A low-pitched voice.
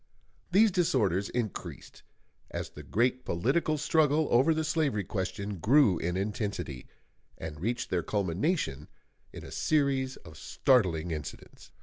Yes: low, 110 Hz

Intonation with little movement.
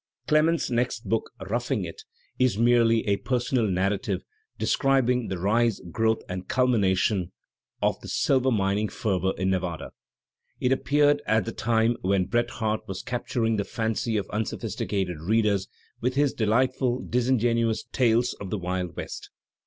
No: average, 3.8 semitones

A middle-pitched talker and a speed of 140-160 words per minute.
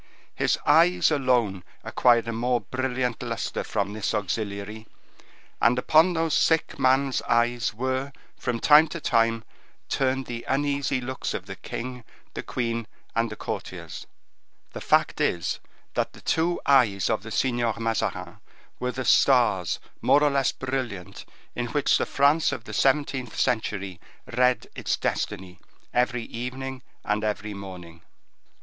No: low, 125 Hz; average, 145 wpm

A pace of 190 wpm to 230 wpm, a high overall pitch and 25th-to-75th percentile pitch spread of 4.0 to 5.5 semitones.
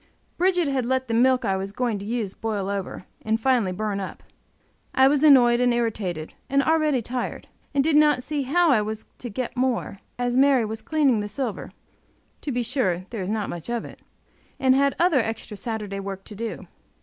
Yes: average, 200 wpm; high, 240 Hz; average, 4.3 semitones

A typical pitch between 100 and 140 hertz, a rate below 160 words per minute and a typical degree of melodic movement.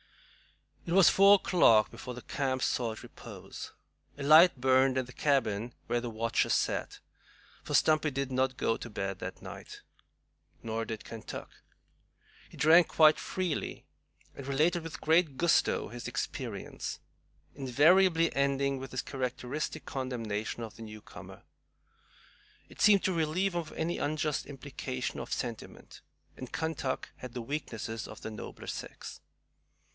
Yes: low, 135 Hz; average, 140 wpm; average, 4.7 semitones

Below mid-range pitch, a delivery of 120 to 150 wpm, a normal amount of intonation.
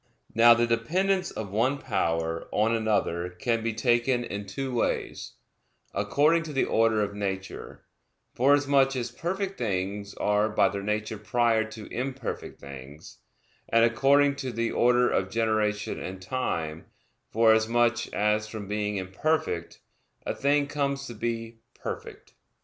Yes: low, 115 Hz; average, 140 wpm; average, 3.9 semitones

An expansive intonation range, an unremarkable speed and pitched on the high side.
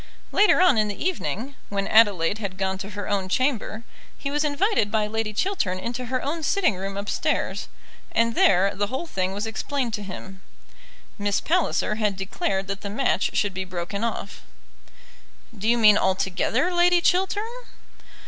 Yes: wide, 5.7 semitones; average, 165 wpm; high, 210 Hz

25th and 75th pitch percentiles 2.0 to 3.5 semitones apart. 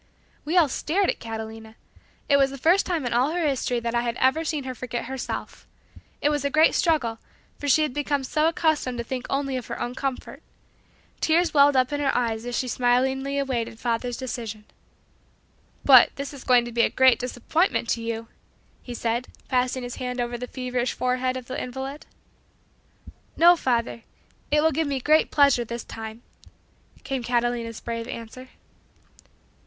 Yes: average, 3.0 semitones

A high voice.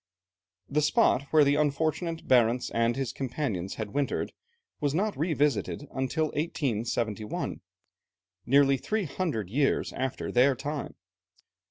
No: medium, 140 Hz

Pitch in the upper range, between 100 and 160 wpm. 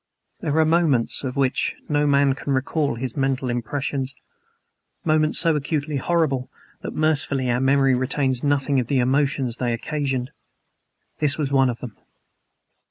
No: low, 135 Hz; average, 150 wpm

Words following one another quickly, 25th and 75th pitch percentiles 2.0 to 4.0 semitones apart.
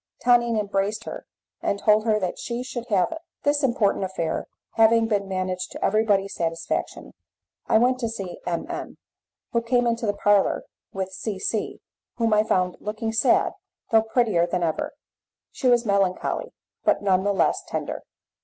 No: average, 165 wpm; average, 3.4 semitones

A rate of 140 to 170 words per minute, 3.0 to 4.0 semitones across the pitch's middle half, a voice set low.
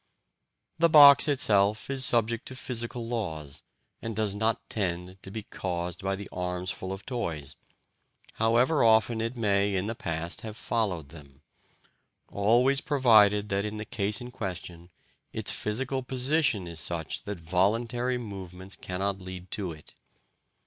No: average, 150 wpm; average, 4.4 semitones; low, 105 Hz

